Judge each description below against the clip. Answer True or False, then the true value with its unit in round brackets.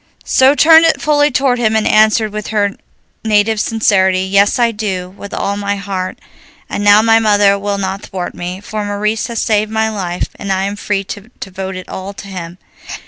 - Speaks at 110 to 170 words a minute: False (195 wpm)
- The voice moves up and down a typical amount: False (2.2 semitones)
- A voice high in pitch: True (205 Hz)